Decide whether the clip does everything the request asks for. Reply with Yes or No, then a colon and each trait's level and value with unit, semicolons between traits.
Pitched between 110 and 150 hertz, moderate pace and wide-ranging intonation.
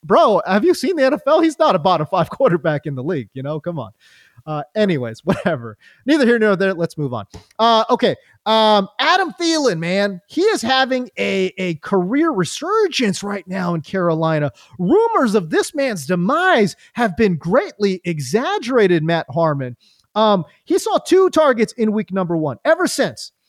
No: high, 200 Hz; average, 175 wpm; wide, 7.8 semitones